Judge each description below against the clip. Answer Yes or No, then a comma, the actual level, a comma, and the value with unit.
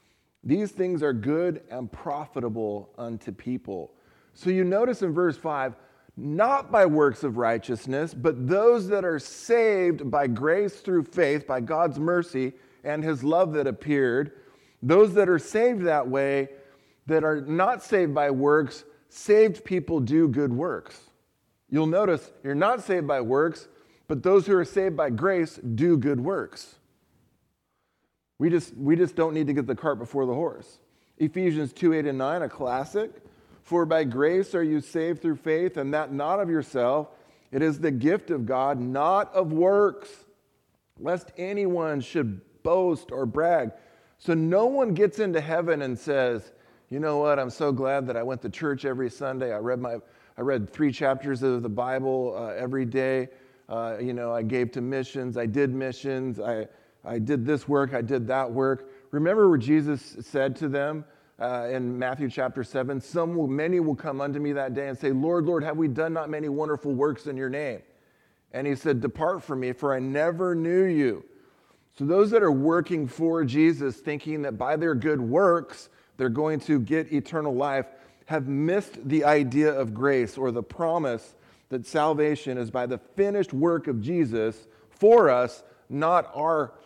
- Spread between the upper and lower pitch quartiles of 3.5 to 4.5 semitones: Yes, average, 4.2 semitones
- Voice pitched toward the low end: No, medium, 145 Hz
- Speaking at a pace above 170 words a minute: Yes, average, 180 wpm